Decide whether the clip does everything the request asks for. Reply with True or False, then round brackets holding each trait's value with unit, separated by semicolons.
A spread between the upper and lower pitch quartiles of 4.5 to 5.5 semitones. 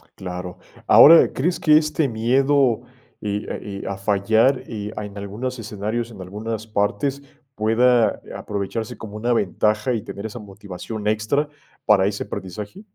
False (3.2 semitones)